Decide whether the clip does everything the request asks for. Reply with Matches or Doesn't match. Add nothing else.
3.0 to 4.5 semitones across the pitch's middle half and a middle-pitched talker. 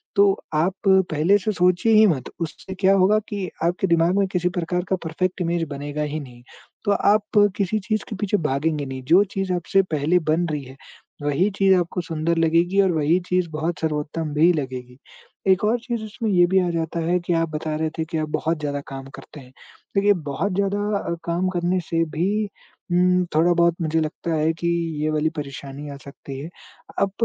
Matches